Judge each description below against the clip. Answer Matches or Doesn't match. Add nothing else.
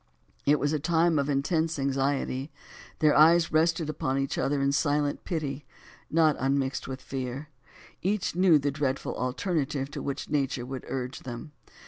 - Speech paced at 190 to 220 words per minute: Doesn't match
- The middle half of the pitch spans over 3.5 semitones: Doesn't match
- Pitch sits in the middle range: Matches